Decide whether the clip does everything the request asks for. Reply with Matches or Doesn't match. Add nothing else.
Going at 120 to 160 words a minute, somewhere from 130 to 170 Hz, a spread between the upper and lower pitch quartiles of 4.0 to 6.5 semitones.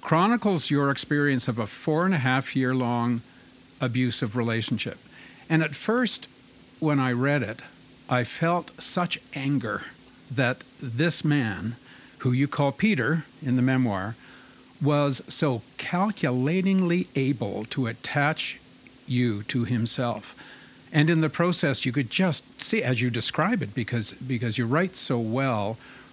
Matches